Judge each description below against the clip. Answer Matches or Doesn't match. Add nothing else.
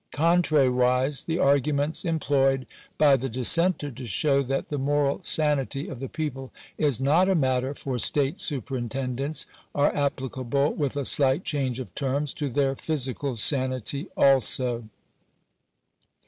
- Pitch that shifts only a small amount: Matches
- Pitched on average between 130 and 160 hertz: Matches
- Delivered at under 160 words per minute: Matches